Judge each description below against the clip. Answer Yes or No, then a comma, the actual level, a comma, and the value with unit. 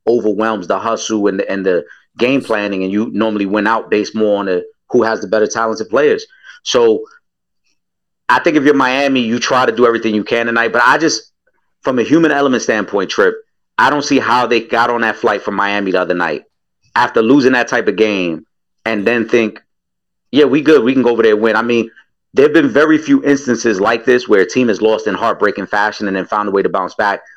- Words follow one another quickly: Yes, fast, 230 wpm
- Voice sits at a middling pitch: No, low, 115 Hz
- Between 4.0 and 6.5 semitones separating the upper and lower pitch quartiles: Yes, average, 4.5 semitones